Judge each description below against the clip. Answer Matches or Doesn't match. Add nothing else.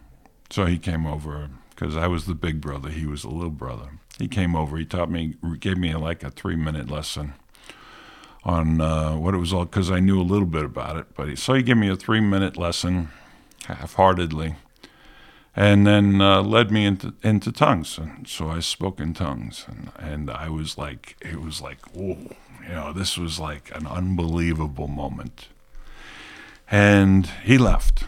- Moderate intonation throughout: Matches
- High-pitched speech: Doesn't match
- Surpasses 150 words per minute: Matches